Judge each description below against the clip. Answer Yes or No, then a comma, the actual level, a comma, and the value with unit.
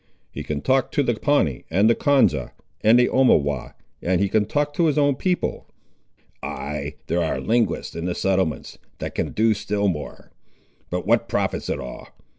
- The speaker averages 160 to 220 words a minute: Yes, average, 180 wpm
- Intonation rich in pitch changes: Yes, wide, 8.0 semitones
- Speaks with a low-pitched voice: Yes, low, 105 Hz